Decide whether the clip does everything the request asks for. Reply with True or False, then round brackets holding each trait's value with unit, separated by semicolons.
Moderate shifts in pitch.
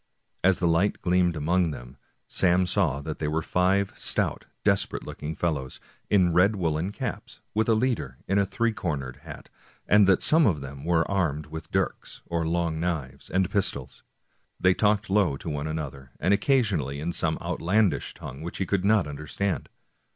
True (4.4 semitones)